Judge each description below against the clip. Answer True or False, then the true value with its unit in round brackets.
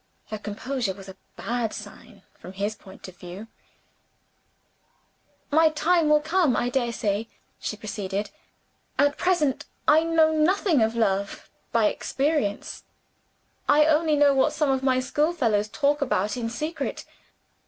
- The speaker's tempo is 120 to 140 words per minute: True (135 wpm)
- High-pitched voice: True (255 Hz)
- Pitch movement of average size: False (6.4 semitones)